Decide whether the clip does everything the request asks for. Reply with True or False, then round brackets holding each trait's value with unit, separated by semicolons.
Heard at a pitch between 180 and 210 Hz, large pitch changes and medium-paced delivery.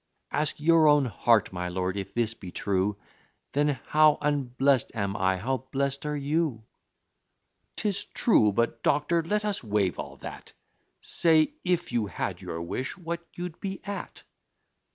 False (140 Hz; 7.5 semitones; 155 wpm)